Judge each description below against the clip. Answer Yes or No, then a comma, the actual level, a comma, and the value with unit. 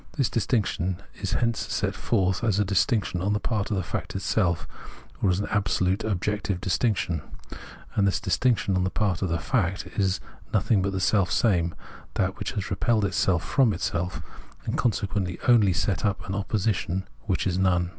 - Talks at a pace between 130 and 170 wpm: No, average, 185 wpm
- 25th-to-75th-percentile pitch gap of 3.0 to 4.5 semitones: No, narrow, 2.6 semitones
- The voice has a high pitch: No, very low, 95 Hz